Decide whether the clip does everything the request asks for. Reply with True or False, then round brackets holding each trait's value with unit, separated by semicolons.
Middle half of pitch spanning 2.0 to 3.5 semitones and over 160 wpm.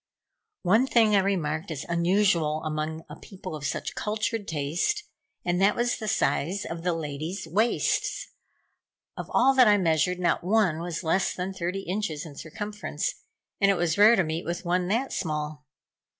False (4.6 semitones; 170 wpm)